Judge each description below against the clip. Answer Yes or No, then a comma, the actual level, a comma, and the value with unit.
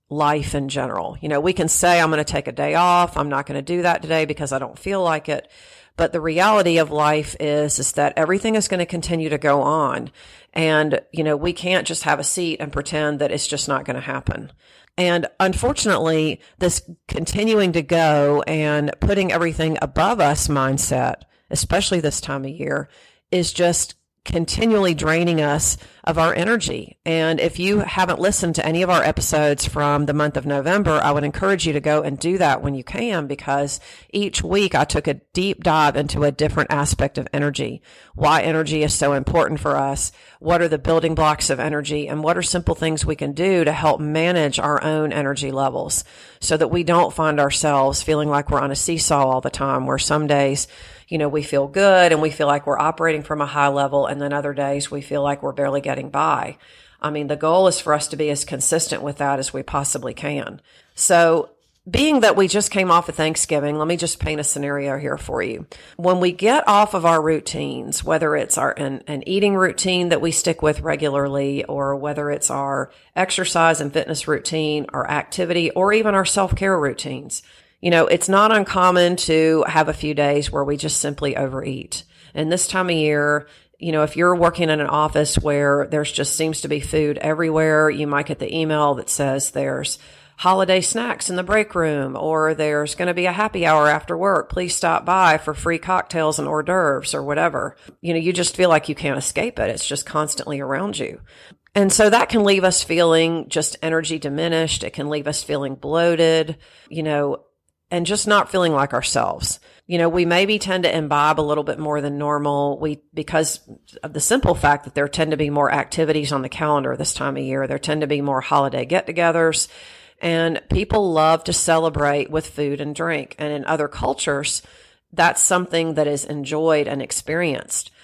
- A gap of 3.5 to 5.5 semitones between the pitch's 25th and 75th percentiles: No, average, 3.0 semitones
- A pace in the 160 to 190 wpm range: No, fast, 205 wpm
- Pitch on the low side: No, medium, 155 Hz